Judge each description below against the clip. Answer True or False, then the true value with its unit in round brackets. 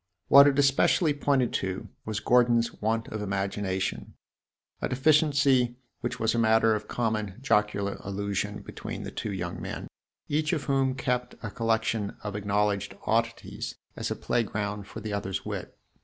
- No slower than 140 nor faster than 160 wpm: True (155 wpm)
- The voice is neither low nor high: False (110 Hz)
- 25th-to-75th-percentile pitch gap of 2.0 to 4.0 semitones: True (3.5 semitones)